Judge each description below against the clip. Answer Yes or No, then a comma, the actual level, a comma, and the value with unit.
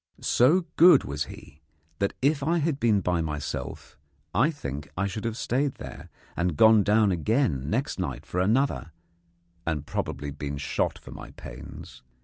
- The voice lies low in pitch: Yes, low, 100 Hz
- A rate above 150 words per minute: Yes, average, 160 wpm